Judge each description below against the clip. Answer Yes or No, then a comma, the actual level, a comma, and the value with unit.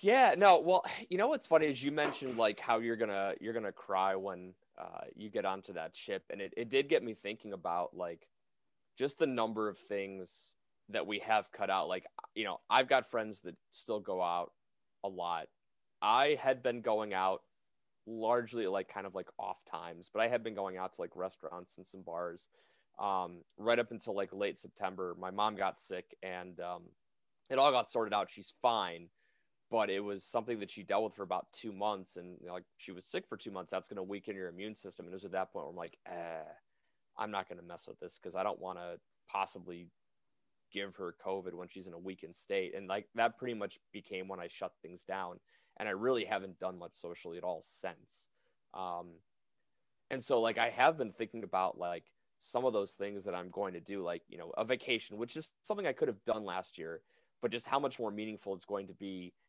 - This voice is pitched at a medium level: No, low, 100 Hz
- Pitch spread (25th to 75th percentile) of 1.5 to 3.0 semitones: No, average, 3.9 semitones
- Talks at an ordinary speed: No, fast, 230 wpm